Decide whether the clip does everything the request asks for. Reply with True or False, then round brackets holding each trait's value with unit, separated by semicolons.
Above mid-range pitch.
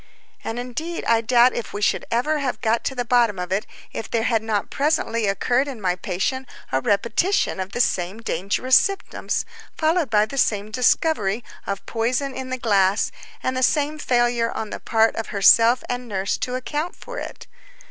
True (235 Hz)